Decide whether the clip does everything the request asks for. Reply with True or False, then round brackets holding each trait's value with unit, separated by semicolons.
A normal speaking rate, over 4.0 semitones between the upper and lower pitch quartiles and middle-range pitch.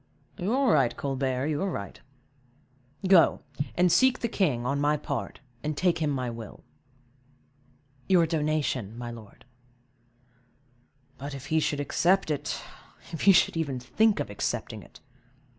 True (145 wpm; 5.6 semitones; 150 Hz)